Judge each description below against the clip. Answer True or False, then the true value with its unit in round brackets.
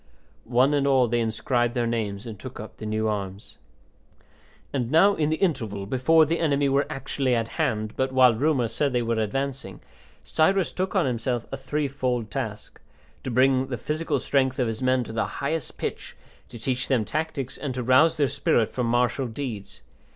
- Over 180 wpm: True (190 wpm)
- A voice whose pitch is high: False (130 Hz)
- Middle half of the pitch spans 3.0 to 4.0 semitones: True (3.5 semitones)